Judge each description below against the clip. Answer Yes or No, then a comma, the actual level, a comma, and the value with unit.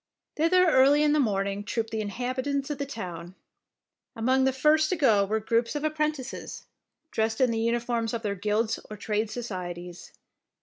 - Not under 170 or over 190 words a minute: Yes, average, 175 wpm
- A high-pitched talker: Yes, high, 230 Hz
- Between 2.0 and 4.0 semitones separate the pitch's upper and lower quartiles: No, average, 4.9 semitones